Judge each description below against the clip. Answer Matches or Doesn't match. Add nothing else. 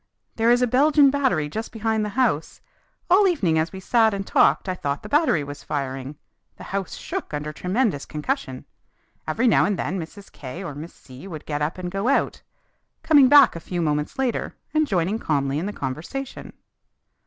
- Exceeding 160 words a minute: Matches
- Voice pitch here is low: Doesn't match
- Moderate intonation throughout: Doesn't match